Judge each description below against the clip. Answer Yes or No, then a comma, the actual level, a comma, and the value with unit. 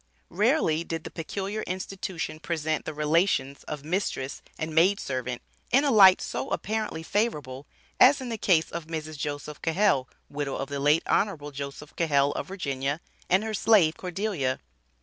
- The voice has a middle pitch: Yes, medium, 160 Hz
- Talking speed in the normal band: Yes, average, 160 wpm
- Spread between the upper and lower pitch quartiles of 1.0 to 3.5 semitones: No, average, 5.3 semitones